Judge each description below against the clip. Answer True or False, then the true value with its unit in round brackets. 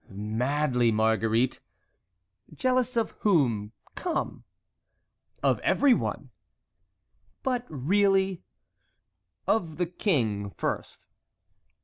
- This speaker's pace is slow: True (70 wpm)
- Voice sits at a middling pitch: True (150 Hz)